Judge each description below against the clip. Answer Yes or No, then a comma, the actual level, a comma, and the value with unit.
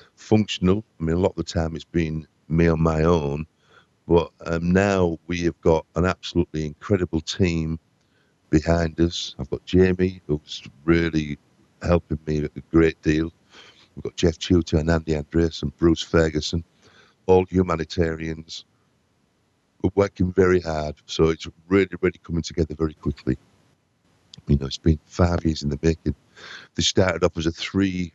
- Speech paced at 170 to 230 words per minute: No, average, 160 wpm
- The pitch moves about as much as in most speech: No, narrow, 2.2 semitones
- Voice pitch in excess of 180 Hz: No, very low, 85 Hz